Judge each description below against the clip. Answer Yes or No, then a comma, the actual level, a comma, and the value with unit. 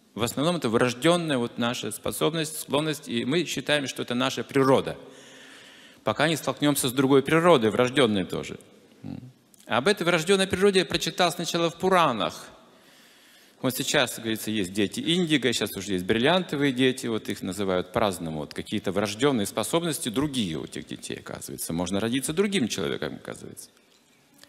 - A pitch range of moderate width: No, wide, 6.8 semitones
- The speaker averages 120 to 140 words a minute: No, average, 155 wpm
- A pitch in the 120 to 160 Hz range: Yes, low, 135 Hz